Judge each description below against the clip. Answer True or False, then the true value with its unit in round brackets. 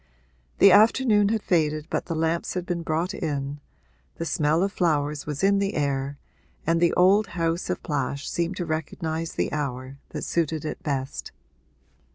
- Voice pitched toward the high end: False (160 Hz)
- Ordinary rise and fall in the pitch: True (3.5 semitones)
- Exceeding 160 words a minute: True (170 wpm)